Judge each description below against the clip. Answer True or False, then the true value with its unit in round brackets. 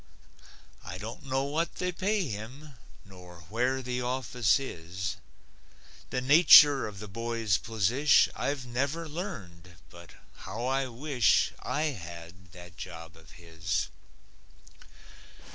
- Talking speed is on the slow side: True (120 wpm)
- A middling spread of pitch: False (7.0 semitones)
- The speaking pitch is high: False (115 Hz)